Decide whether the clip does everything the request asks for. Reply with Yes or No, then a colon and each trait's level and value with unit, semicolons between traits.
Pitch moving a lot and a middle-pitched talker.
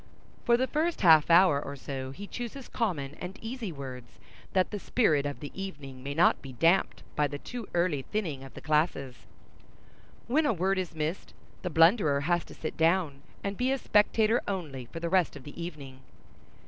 Yes: wide, 5.9 semitones; medium, 170 Hz